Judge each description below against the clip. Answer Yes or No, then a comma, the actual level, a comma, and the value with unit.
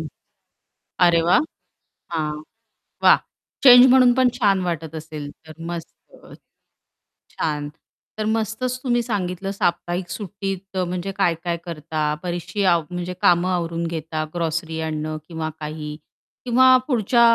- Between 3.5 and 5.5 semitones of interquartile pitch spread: Yes, average, 4.0 semitones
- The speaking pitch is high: No, medium, 175 Hz